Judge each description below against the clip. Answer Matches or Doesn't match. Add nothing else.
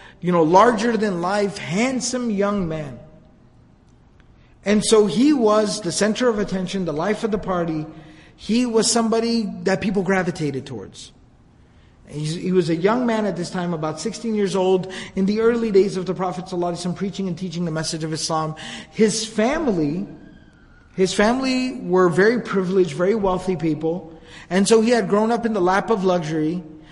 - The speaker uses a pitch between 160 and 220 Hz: Matches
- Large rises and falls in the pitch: Doesn't match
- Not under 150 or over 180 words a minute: Matches